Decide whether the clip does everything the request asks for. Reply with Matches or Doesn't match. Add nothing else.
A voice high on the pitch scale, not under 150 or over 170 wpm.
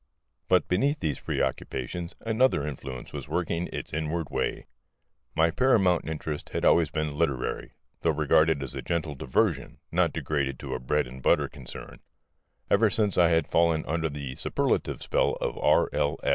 Doesn't match